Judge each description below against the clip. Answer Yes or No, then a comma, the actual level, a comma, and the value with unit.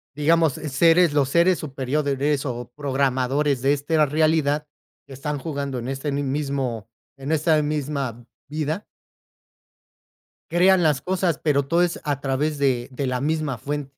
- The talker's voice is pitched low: No, medium, 145 Hz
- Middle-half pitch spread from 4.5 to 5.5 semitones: No, narrow, 2.4 semitones